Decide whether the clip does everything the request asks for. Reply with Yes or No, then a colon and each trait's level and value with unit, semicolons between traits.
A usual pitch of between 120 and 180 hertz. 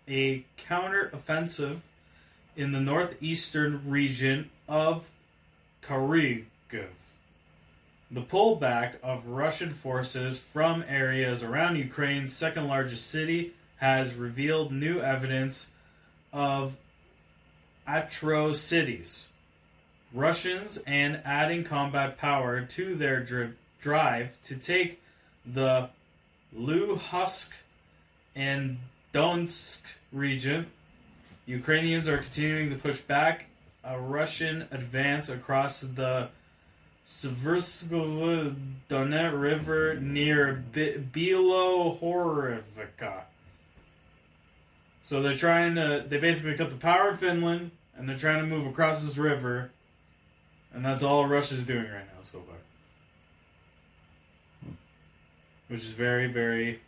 Yes: low, 135 Hz